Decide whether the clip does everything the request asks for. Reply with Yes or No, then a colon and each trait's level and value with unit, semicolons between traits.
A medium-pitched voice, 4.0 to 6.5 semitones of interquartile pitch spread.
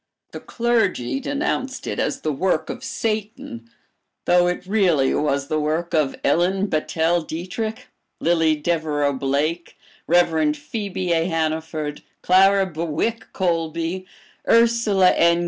Yes: medium, 175 Hz; average, 4.3 semitones